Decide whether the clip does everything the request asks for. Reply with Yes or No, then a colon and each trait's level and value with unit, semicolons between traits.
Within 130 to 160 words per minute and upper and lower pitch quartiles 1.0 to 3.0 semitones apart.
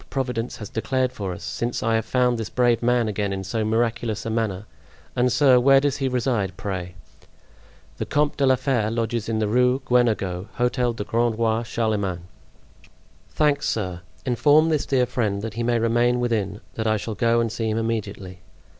No: average, 190 wpm; average, 2.7 semitones